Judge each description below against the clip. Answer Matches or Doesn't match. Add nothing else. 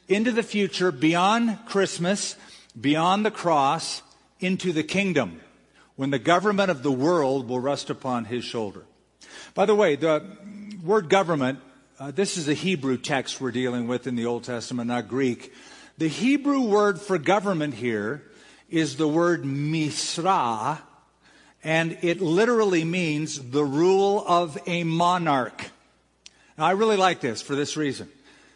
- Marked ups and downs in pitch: Matches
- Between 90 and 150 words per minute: Matches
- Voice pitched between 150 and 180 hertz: Matches